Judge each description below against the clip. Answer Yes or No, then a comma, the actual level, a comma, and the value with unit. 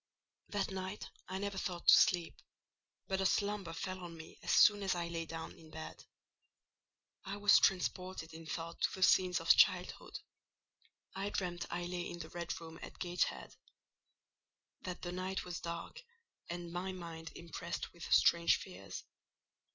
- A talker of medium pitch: Yes, medium, 175 Hz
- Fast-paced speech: No, average, 160 wpm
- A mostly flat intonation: Yes, narrow, 2.0 semitones